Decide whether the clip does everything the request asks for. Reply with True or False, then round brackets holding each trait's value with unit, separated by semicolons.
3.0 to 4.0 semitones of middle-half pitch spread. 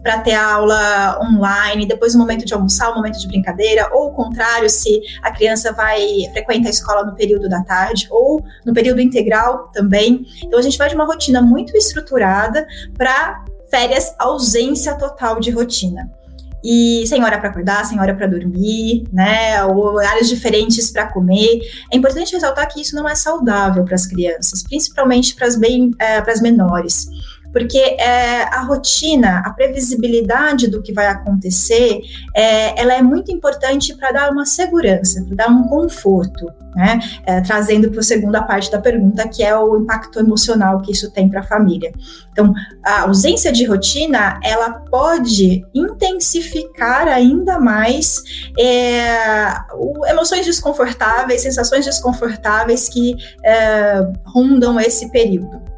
True (3.6 semitones)